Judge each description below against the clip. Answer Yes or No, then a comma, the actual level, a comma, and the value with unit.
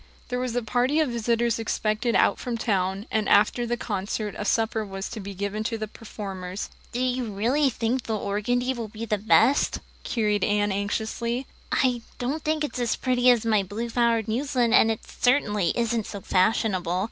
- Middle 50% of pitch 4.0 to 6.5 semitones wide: No, average, 2.9 semitones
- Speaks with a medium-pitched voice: No, high, 225 Hz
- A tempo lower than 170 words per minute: No, average, 180 wpm